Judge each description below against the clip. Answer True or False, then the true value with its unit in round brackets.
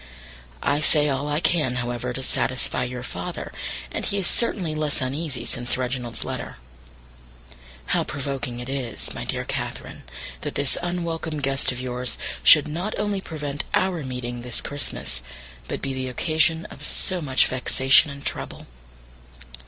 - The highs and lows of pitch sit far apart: False (3.9 semitones)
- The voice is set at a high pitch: False (140 Hz)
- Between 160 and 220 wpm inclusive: False (150 wpm)